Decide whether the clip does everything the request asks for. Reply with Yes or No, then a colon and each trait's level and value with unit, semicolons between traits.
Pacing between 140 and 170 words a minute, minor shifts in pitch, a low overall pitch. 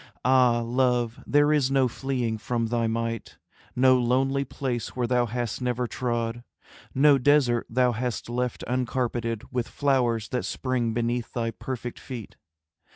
Yes: average, 145 wpm; narrow, 1.7 semitones; low, 125 Hz